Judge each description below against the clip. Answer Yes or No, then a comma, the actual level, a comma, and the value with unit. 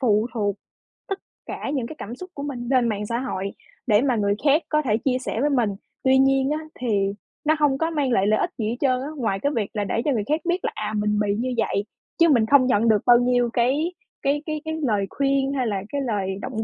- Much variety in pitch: No, average, 4.7 semitones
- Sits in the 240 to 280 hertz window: Yes, very high, 250 Hz